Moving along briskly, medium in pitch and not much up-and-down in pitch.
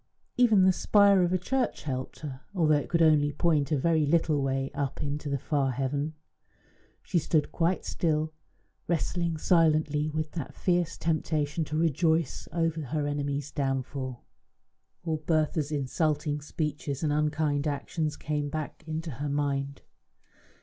No: average, 145 wpm; medium, 150 Hz; narrow, 2.3 semitones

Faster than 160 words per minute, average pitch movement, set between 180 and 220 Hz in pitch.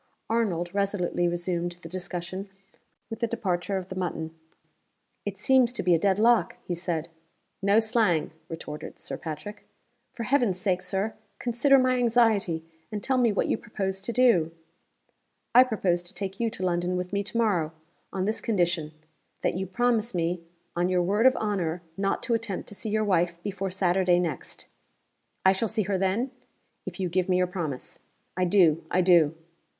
Yes: average, 175 wpm; average, 3.9 semitones; high, 190 Hz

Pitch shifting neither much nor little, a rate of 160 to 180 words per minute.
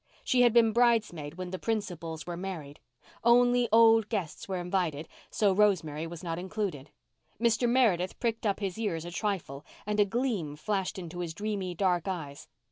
Yes: average, 4.6 semitones; average, 170 wpm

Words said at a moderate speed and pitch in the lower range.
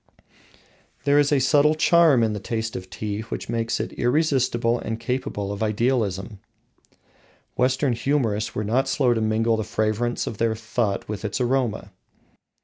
Yes: average, 155 wpm; low, 115 Hz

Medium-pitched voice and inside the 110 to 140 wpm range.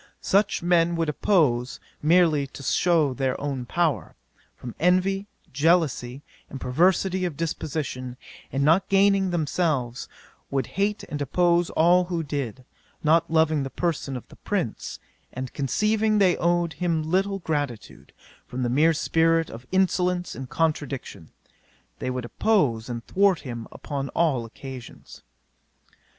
Yes: medium, 160 Hz; slow, 135 wpm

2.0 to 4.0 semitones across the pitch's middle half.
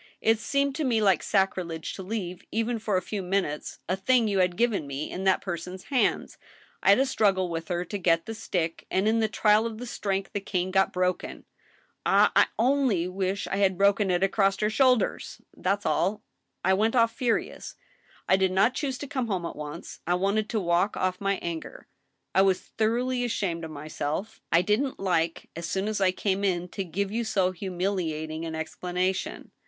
Yes: average, 3.5 semitones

